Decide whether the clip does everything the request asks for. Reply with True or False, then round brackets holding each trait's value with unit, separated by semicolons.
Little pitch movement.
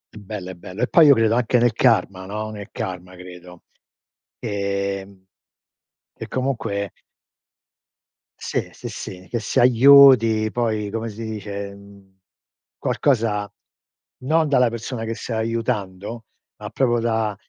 False (3.0 semitones)